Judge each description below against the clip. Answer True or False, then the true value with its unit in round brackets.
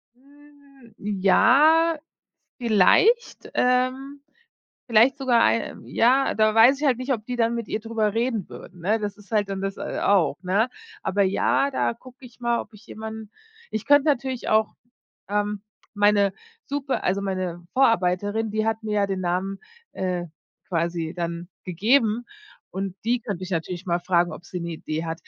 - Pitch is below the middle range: False (215 Hz)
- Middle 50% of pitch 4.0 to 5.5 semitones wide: True (4.9 semitones)